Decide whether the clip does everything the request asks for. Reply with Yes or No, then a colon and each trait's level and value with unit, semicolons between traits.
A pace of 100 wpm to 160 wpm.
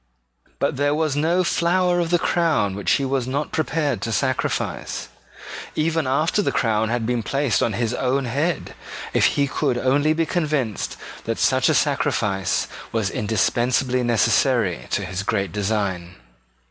Yes: average, 155 wpm